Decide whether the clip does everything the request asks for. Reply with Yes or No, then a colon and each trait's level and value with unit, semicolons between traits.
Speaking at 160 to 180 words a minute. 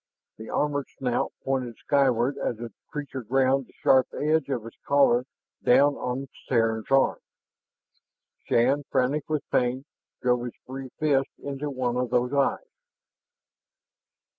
No: average, 140 wpm